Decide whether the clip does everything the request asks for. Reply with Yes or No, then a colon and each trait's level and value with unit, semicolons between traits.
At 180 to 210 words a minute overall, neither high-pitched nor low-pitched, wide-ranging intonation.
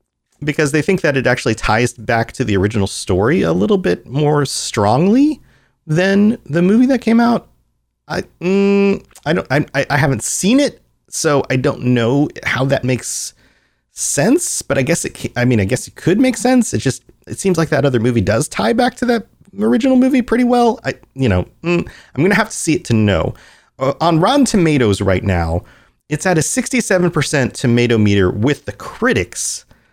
Yes: average, 190 wpm; medium, 145 Hz; wide, 8.6 semitones